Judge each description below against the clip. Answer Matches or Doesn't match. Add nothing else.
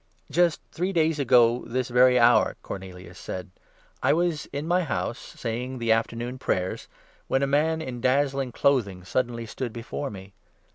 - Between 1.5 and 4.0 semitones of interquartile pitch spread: Matches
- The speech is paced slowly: Doesn't match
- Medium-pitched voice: Doesn't match